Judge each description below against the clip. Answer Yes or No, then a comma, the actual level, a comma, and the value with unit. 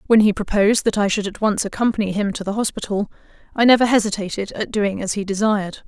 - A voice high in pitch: Yes, high, 205 Hz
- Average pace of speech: No, fast, 215 wpm